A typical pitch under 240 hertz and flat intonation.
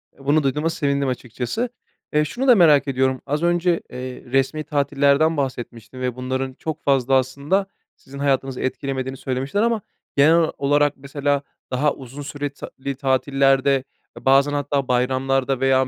Yes: medium, 140 Hz; narrow, 1.8 semitones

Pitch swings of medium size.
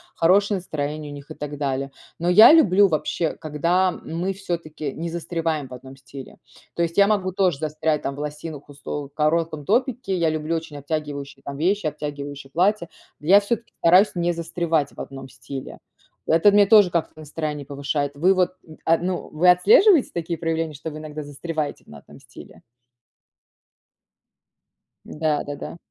Yes: average, 3.6 semitones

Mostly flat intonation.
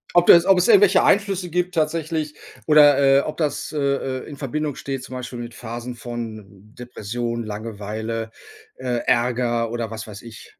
No: average, 4.7 semitones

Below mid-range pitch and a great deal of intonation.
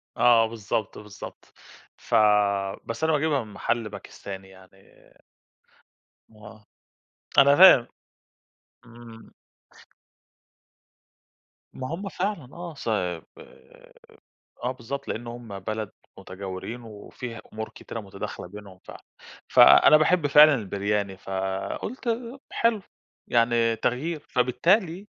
Yes: low, 115 Hz; wide, 6.2 semitones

